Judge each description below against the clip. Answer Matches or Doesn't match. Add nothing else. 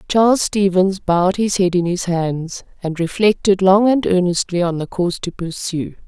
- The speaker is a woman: Matches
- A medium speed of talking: Matches